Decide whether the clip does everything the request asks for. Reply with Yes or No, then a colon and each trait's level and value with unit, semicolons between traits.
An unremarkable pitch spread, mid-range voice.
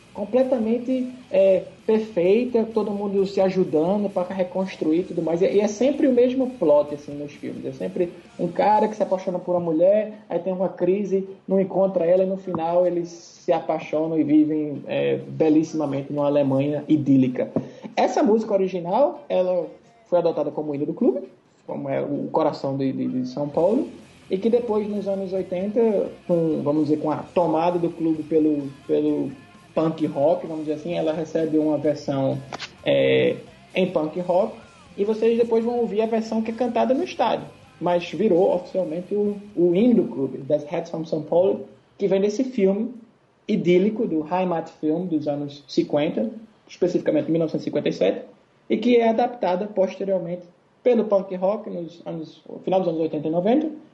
Yes: average, 4.8 semitones; medium, 180 Hz